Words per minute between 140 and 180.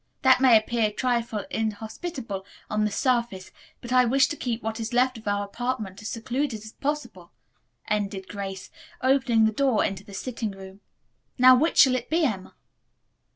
Yes: average, 175 wpm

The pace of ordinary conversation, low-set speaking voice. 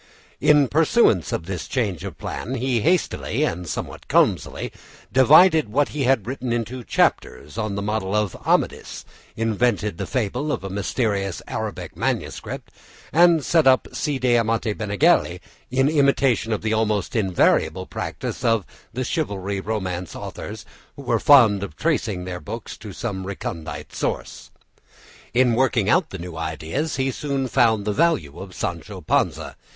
Yes: average, 150 wpm; low, 110 Hz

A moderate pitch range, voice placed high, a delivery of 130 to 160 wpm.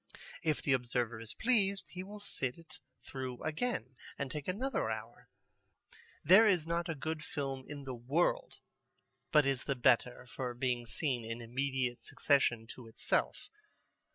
No: average, 4.8 semitones; low, 135 Hz; average, 155 wpm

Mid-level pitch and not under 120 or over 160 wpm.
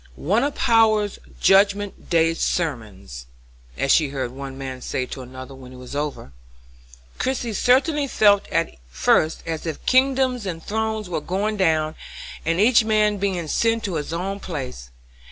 Yes: medium, 175 Hz; average, 155 wpm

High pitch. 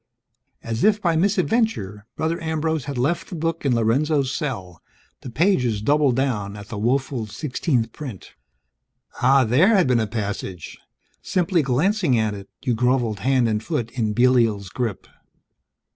No: low, 125 Hz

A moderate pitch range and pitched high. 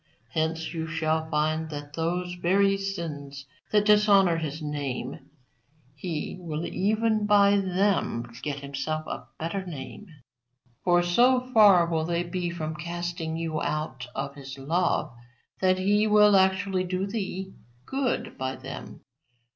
No: average, 4.0 semitones; medium, 175 Hz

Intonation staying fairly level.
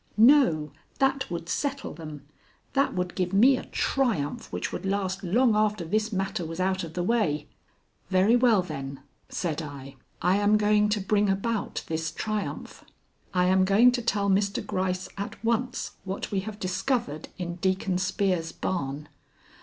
No: average, 3.8 semitones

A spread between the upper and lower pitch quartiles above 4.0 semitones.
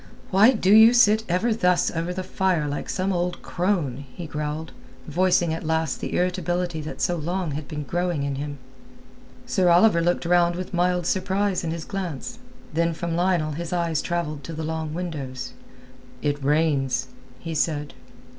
No: average, 2.9 semitones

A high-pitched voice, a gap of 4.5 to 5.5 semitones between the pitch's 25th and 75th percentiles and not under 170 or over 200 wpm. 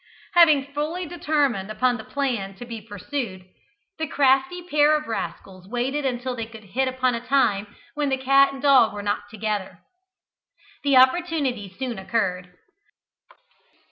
No: very high, 255 Hz; average, 5.0 semitones; average, 145 wpm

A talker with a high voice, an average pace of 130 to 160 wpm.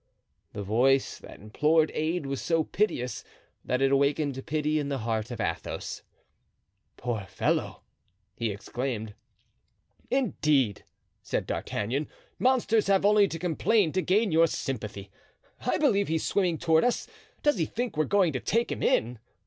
No: medium, 150 Hz; average, 150 wpm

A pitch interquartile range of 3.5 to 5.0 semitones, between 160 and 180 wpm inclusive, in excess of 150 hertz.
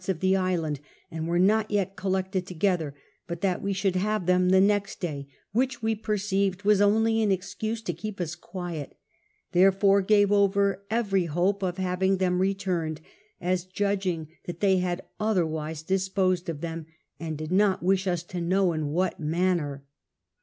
No: narrow, 2.4 semitones; average, 170 wpm; medium, 185 Hz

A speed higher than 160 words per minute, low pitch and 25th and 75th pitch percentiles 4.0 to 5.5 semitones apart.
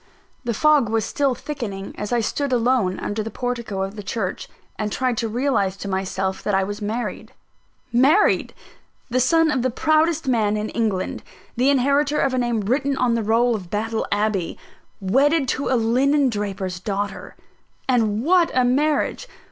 No: average, 170 wpm; high, 235 Hz; average, 4.6 semitones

